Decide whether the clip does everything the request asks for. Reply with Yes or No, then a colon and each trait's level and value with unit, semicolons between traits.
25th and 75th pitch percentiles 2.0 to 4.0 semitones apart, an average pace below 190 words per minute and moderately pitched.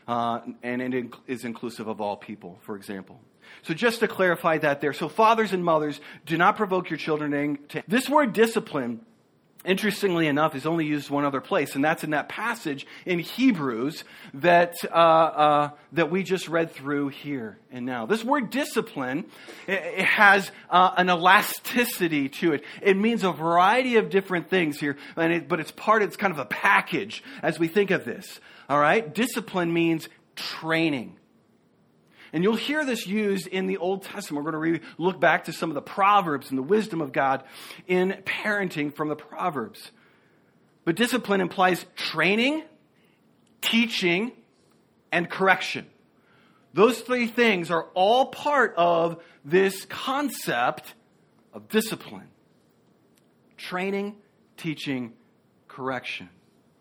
No: wide, 5.4 semitones; average, 150 wpm; medium, 175 Hz